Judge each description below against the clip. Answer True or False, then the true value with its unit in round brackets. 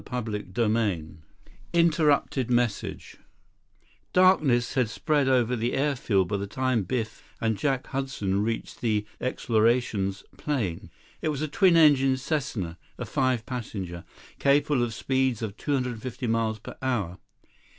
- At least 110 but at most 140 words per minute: True (135 wpm)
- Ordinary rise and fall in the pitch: True (3.9 semitones)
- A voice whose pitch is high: False (120 Hz)